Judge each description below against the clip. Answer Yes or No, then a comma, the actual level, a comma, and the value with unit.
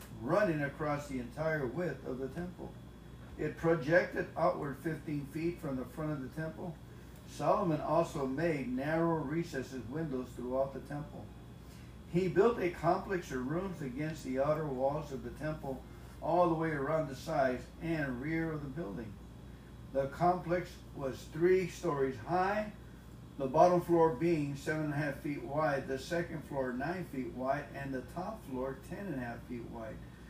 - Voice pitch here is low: No, medium, 145 Hz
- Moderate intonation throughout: Yes, average, 4.1 semitones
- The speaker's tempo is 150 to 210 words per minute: Yes, average, 165 wpm